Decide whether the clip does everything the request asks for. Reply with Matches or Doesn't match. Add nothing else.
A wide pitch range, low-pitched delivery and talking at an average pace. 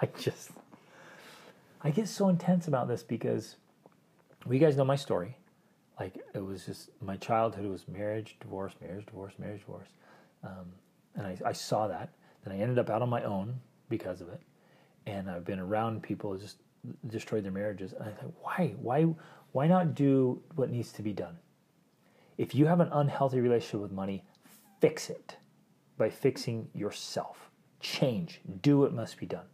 Matches